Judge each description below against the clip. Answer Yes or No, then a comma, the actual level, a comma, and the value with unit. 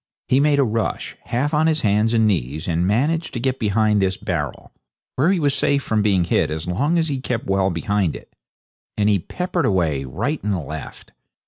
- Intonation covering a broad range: Yes, wide, 7.0 semitones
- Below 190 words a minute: No, fast, 205 wpm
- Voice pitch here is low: Yes, low, 110 Hz